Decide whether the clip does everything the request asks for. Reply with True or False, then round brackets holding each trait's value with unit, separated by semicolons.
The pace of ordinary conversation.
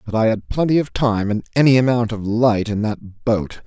False (230 wpm)